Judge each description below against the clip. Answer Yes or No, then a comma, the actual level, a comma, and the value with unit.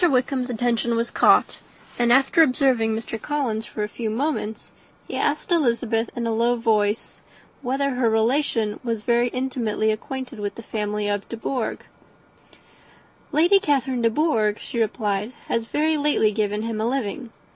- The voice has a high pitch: Yes, high, 235 Hz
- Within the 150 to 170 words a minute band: Yes, average, 155 wpm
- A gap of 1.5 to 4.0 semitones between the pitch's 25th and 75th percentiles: Yes, average, 3.3 semitones